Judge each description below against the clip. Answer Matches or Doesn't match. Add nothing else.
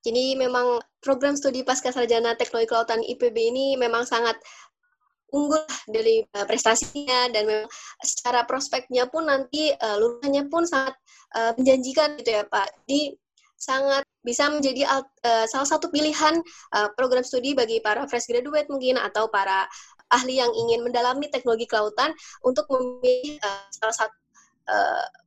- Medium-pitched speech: Doesn't match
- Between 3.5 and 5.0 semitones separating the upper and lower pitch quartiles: Matches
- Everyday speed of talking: Doesn't match